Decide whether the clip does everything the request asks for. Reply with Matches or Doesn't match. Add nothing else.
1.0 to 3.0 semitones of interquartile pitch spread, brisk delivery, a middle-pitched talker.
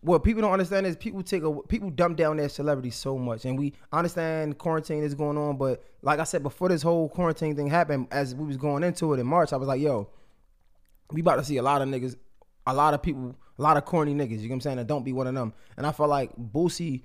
Doesn't match